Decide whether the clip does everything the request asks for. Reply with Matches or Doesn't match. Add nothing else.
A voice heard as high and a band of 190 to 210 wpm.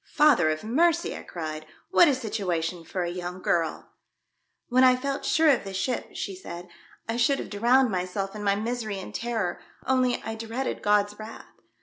Matches